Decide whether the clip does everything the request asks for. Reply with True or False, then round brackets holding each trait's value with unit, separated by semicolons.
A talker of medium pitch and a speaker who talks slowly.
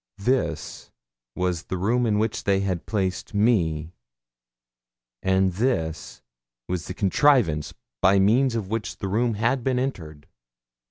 False (100 Hz; 125 wpm)